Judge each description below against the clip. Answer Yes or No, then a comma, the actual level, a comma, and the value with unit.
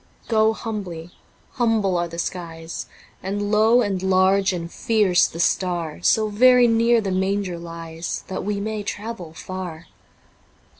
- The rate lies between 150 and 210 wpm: No, average, 140 wpm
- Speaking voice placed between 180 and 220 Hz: Yes, high, 190 Hz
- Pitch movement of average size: Yes, average, 3.9 semitones